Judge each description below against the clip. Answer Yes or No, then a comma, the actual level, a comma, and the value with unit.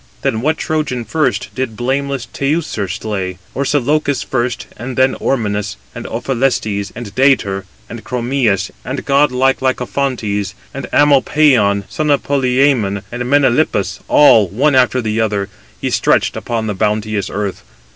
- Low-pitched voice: Yes, low, 125 Hz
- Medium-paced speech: No, slow, 125 wpm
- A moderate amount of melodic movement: Yes, average, 4.7 semitones